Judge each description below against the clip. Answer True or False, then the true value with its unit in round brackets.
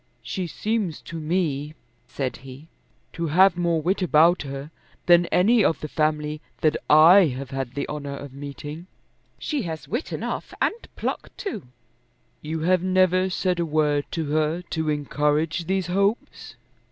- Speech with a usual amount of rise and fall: True (3.5 semitones)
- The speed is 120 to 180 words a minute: True (155 wpm)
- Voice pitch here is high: False (160 Hz)